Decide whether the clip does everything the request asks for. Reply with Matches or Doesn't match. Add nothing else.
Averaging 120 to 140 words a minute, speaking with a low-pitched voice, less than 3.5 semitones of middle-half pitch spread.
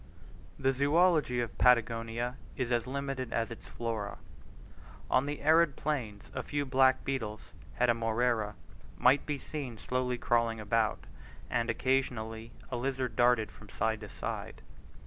Matches